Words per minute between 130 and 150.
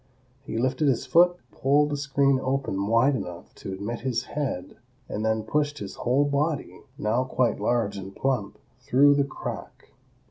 No: average, 165 wpm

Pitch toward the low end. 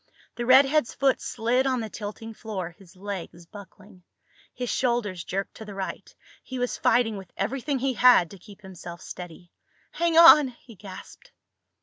No: high, 220 Hz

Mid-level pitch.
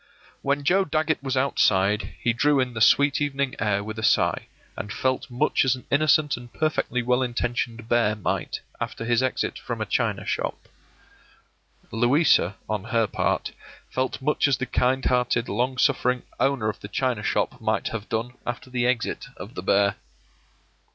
No: low, 125 Hz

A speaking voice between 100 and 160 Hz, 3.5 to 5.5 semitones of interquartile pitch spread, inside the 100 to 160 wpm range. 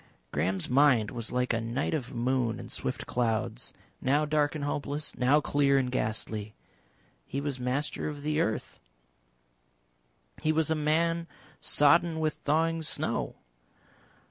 Yes: medium, 140 Hz; average, 3.8 semitones; average, 140 wpm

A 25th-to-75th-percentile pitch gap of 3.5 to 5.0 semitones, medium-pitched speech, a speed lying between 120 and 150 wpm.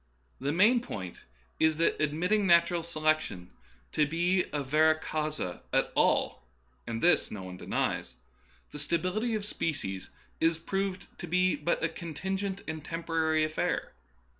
No: average, 3.1 semitones; medium, 165 Hz; average, 145 wpm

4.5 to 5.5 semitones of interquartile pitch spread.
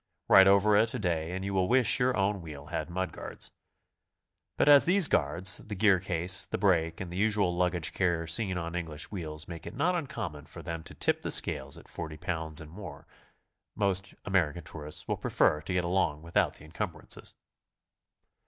No: average, 3.5 semitones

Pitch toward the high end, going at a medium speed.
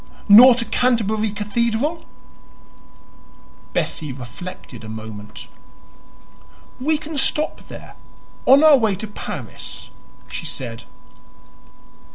No: high, 220 Hz; slow, 95 wpm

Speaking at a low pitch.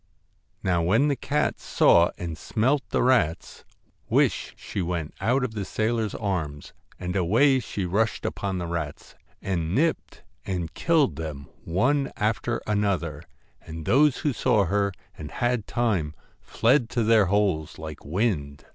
Yes: low, 100 Hz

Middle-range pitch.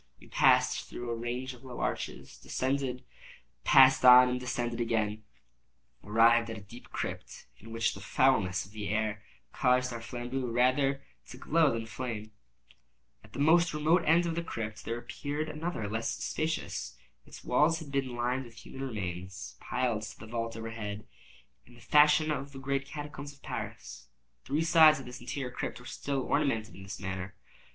No: low, 125 Hz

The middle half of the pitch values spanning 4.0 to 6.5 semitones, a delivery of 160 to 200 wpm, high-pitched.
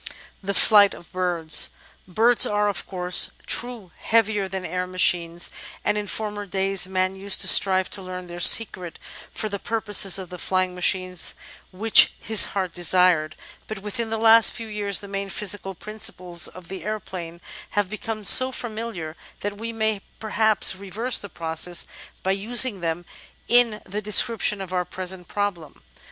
No: average, 2.8 semitones; average, 165 wpm; high, 195 Hz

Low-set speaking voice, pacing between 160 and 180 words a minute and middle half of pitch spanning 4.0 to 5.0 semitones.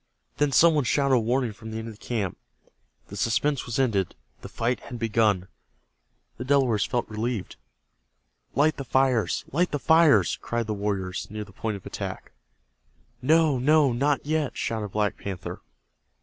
Yes: low, 120 Hz; average, 165 wpm; average, 4.6 semitones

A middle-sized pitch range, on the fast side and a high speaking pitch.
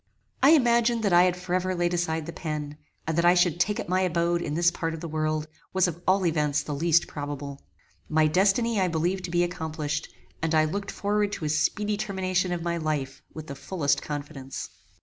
No: average, 3.1 semitones; fast, 215 wpm; medium, 170 Hz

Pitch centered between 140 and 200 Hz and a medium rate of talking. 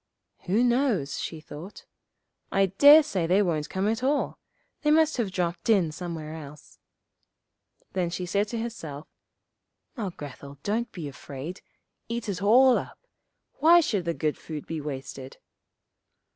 Yes: medium, 185 Hz; average, 145 wpm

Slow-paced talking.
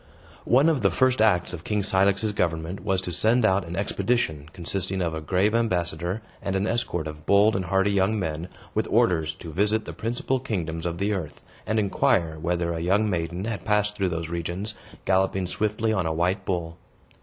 No: average, 195 wpm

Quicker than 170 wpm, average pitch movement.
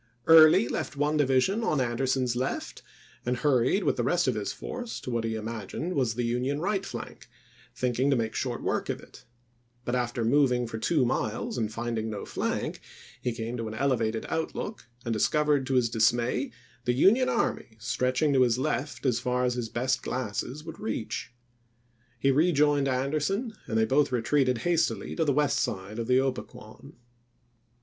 Yes: average, 180 wpm; average, 3.8 semitones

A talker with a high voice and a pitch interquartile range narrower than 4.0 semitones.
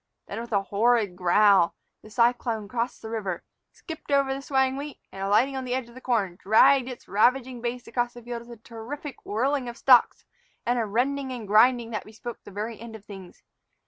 Yes: high, 235 Hz; average, 3.3 semitones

